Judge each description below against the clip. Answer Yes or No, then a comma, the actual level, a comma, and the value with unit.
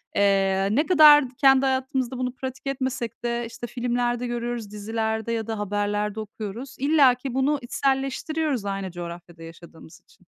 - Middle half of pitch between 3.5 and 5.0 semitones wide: Yes, average, 4.2 semitones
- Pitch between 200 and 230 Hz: No, high, 240 Hz